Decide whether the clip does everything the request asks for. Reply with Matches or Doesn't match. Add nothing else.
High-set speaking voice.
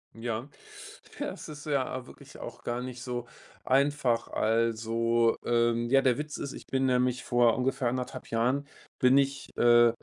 Doesn't match